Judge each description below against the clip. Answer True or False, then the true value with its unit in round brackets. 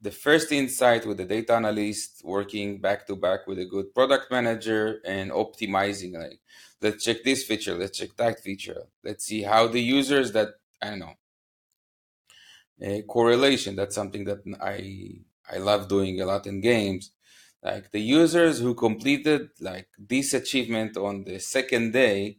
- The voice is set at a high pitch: False (105 Hz)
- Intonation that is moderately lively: True (3.7 semitones)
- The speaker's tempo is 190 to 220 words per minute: False (165 wpm)